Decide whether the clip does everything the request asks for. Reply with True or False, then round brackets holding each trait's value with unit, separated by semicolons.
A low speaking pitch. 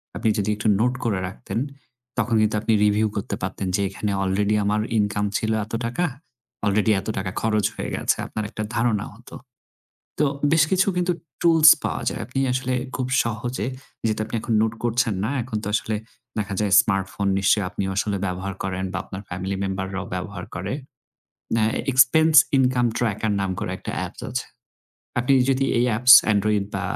True (105 Hz)